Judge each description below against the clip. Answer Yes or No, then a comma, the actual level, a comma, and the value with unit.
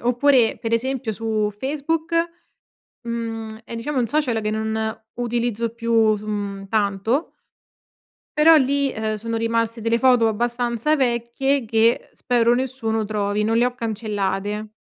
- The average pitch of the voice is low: No, high, 230 Hz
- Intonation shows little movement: Yes, narrow, 2.2 semitones